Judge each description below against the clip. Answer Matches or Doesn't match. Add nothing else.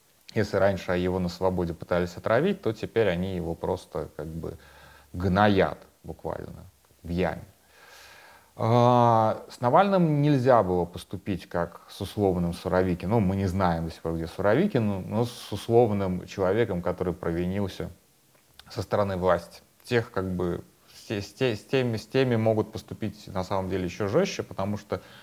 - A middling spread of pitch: Matches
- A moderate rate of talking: Matches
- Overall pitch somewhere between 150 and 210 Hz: Doesn't match